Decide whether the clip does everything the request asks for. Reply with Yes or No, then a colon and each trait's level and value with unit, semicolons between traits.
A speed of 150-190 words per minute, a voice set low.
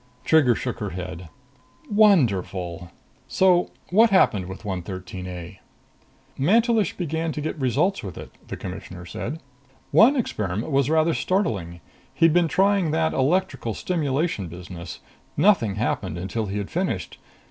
No: slow, 135 wpm; low, 130 Hz